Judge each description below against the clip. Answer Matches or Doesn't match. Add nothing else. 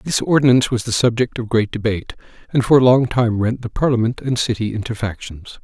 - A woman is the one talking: Doesn't match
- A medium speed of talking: Doesn't match